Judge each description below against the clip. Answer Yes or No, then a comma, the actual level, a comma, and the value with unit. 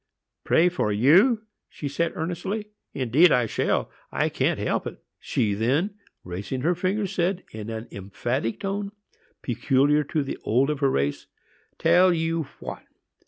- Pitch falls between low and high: Yes, medium, 150 Hz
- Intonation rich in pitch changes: Yes, wide, 7.2 semitones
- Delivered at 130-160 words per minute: Yes, average, 145 wpm